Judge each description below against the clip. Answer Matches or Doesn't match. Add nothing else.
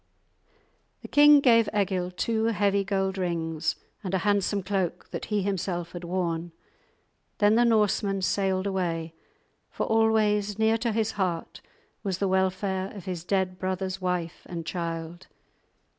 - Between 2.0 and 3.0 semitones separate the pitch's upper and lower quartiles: Matches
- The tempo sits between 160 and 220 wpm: Doesn't match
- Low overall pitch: Doesn't match